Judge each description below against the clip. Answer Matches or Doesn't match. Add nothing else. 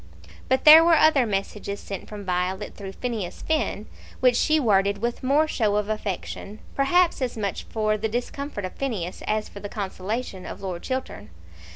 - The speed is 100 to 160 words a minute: Doesn't match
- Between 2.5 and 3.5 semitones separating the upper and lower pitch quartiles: Doesn't match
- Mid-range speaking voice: Doesn't match